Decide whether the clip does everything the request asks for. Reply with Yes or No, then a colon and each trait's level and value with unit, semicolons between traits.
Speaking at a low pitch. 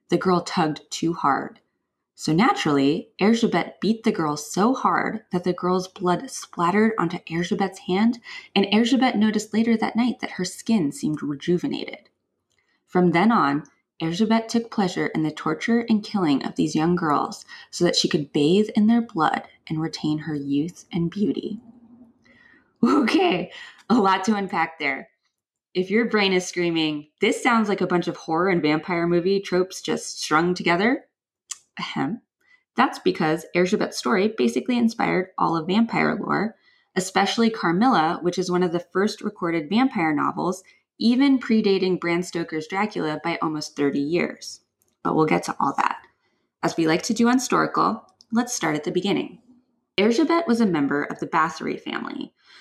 No: medium, 185 Hz